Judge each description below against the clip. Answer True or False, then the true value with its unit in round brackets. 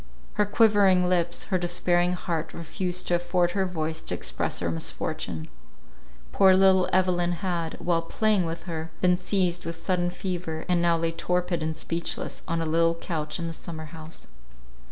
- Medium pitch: True (175 Hz)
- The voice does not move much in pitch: True (1.8 semitones)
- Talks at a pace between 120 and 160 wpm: False (170 wpm)